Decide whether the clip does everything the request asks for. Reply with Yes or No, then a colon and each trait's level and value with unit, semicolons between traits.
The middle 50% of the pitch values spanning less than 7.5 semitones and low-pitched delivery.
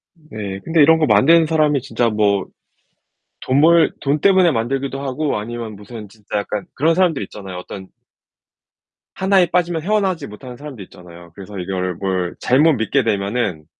No: wide, 7.8 semitones; low, 125 Hz